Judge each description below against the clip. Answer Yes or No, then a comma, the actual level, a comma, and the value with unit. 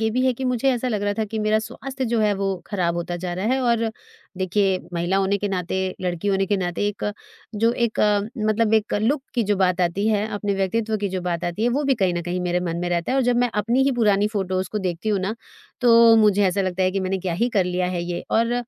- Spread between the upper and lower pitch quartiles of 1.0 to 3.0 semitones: No, average, 3.6 semitones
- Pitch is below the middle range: No, high, 205 Hz